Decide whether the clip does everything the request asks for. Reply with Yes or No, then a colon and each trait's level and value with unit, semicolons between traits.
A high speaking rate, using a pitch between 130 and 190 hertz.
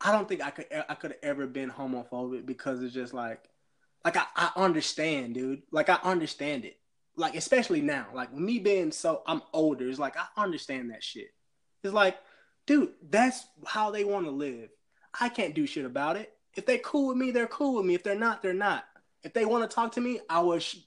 Yes: fast, 225 wpm; medium, 185 Hz